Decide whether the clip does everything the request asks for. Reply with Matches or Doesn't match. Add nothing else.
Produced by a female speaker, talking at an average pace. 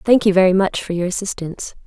Doesn't match